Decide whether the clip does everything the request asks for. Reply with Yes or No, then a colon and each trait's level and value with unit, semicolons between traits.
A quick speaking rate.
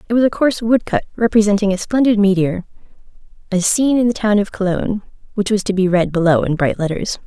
Yes: fast, 215 wpm